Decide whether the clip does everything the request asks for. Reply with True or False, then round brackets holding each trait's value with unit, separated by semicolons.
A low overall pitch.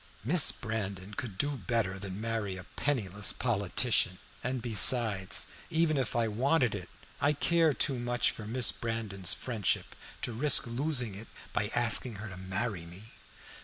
True (115 Hz)